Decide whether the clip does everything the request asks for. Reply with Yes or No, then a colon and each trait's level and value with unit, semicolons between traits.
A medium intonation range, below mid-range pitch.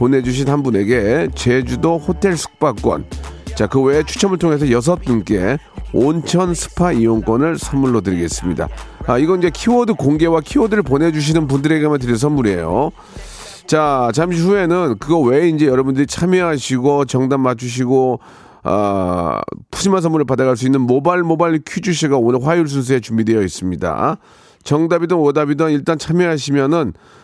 No: average, 5.0 semitones; medium, 145 Hz